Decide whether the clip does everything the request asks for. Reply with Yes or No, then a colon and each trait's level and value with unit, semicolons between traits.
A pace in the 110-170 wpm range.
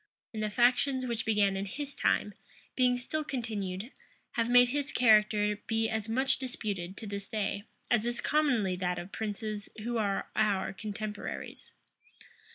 Yes: average, 155 wpm